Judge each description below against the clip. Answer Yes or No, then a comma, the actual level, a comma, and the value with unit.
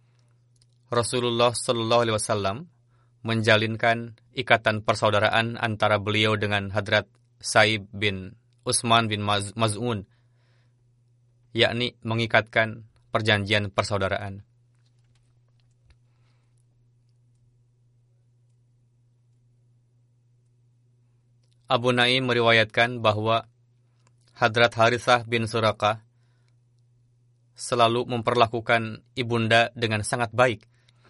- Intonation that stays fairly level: Yes, narrow, 1.2 semitones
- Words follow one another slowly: Yes, slow, 65 wpm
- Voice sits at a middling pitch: No, low, 120 Hz